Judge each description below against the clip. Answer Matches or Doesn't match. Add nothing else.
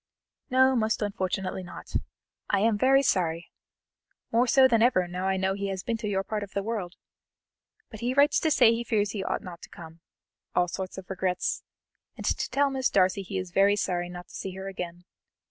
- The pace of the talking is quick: Matches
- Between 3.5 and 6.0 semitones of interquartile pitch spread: Matches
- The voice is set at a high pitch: Matches